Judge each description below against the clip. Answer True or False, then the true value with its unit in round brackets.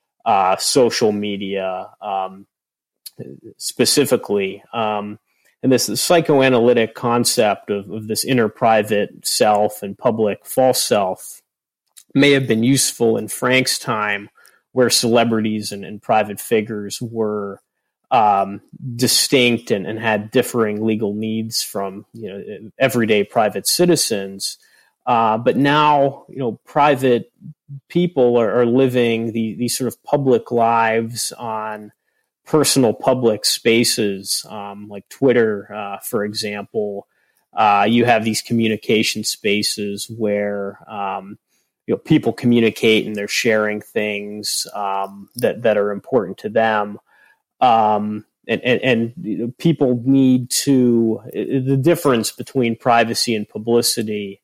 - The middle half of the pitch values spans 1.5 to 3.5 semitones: True (3.1 semitones)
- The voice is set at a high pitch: False (115 Hz)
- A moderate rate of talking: False (120 wpm)